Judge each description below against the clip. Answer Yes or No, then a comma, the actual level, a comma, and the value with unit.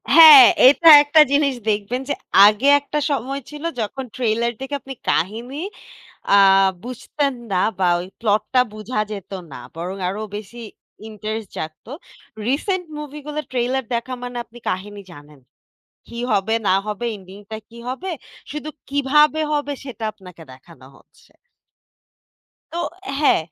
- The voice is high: Yes, high, 240 Hz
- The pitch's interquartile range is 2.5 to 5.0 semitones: No, wide, 5.5 semitones